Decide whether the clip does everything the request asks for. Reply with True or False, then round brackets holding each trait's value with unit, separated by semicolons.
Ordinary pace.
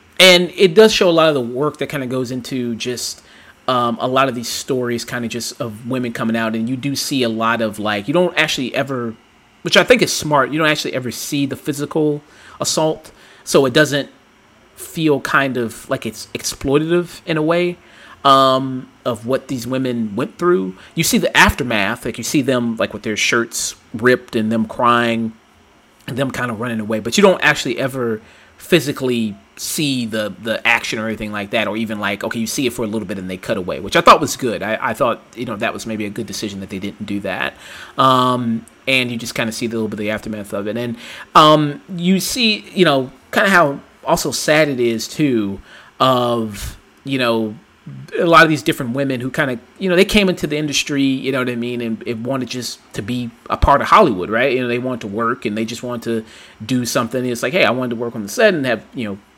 False (235 wpm)